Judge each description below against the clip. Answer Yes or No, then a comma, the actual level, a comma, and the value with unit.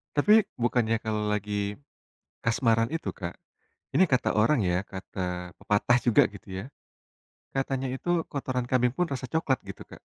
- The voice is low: Yes, low, 120 Hz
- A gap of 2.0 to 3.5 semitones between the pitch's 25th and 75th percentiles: No, average, 4.1 semitones